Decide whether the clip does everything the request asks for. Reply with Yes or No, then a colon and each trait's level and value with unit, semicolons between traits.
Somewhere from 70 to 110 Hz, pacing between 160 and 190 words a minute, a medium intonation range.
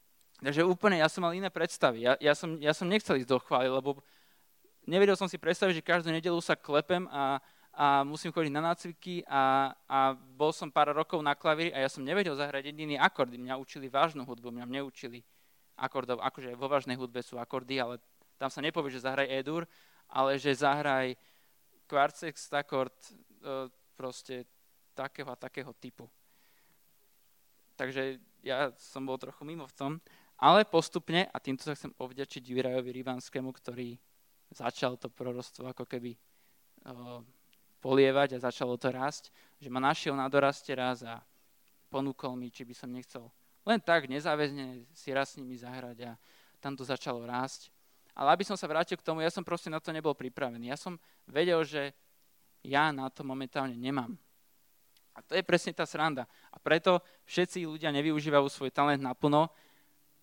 No: medium, 140 Hz; fast, 165 wpm; average, 3.5 semitones